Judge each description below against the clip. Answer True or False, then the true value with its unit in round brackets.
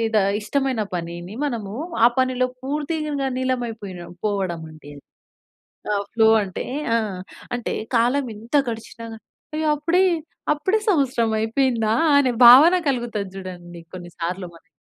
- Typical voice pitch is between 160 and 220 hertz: False (230 Hz)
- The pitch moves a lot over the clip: True (5.9 semitones)